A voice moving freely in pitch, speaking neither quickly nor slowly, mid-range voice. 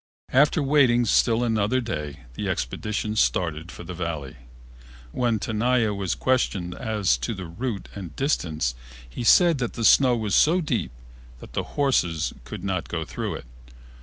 No: wide, 6.2 semitones; average, 160 wpm; low, 105 Hz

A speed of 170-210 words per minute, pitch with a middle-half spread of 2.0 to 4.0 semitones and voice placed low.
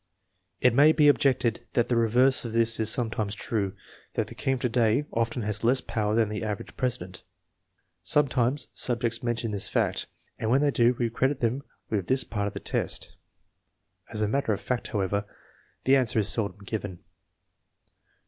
Yes: average, 180 wpm; average, 3.1 semitones; low, 115 Hz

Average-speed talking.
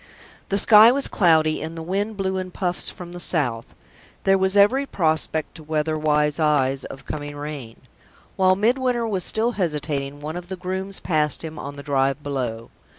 Yes: average, 180 wpm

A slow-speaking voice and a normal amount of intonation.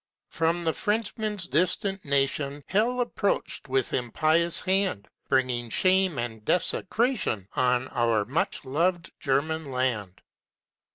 No: slow, 110 wpm; wide, 6.7 semitones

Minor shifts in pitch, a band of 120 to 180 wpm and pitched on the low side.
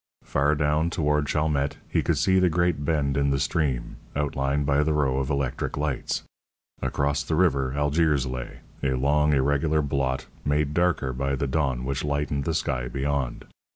Yes: narrow, 1.8 semitones; average, 170 wpm; very low, 70 Hz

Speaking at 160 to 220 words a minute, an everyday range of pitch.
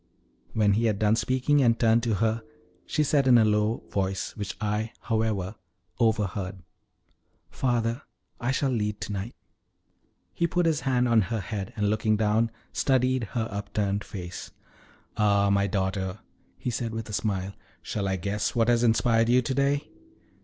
Yes: average, 165 wpm; average, 3.0 semitones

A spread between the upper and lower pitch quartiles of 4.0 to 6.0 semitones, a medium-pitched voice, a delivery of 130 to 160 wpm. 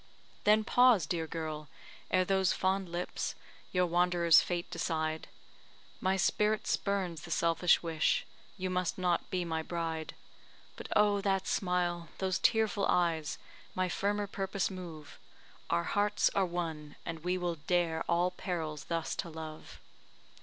No: average, 2.7 semitones; medium, 175 Hz; average, 140 wpm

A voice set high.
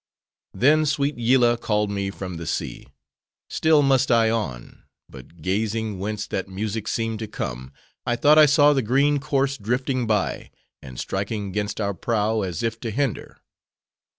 No: low, 110 Hz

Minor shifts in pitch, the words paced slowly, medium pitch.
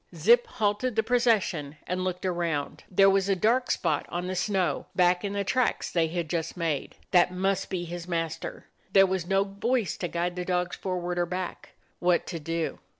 No: narrow, 2.2 semitones; average, 195 wpm; medium, 180 Hz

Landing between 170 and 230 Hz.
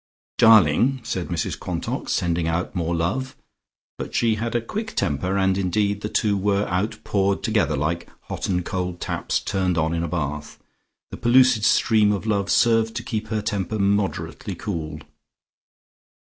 No: low, 100 Hz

